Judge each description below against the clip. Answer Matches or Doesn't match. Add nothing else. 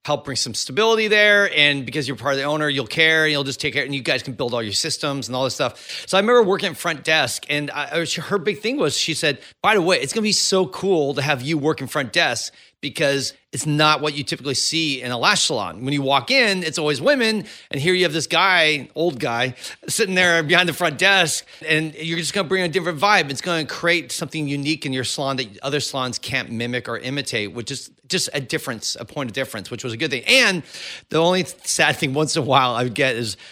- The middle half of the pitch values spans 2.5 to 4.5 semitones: Matches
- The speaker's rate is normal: Doesn't match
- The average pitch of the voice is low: Doesn't match